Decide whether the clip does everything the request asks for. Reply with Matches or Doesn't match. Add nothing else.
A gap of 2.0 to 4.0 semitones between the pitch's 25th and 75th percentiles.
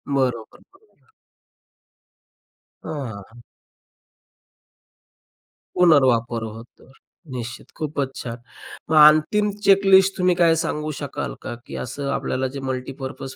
Doesn't match